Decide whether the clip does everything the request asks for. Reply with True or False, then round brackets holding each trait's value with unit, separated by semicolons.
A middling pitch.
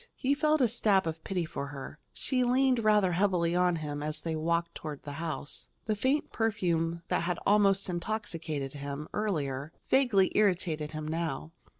True (170 Hz)